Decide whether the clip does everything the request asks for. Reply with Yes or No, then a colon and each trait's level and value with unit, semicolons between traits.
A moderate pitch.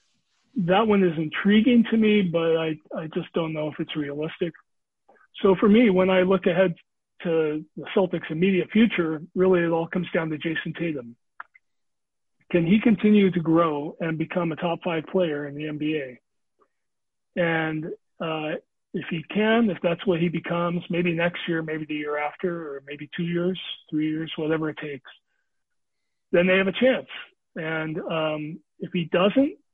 Yes: medium, 170 Hz